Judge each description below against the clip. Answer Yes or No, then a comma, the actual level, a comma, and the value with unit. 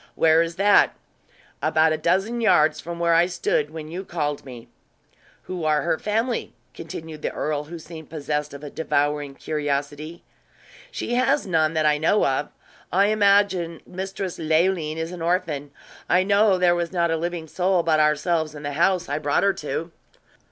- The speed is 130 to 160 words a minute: No, average, 175 wpm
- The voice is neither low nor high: Yes, medium, 165 Hz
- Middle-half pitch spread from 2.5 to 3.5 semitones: Yes, average, 3.1 semitones